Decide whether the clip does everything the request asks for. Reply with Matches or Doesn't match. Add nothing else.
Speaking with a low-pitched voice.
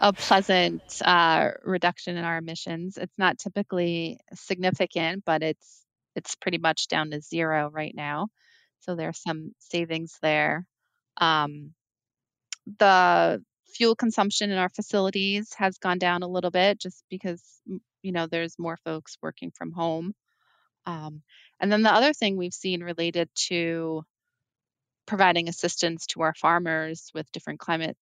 Doesn't match